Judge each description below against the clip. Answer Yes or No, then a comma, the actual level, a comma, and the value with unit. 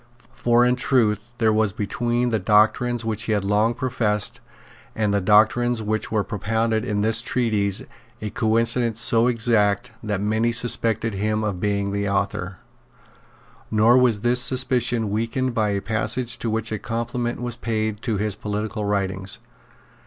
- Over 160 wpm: No, average, 155 wpm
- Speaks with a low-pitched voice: Yes, low, 110 Hz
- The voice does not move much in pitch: Yes, narrow, 2.2 semitones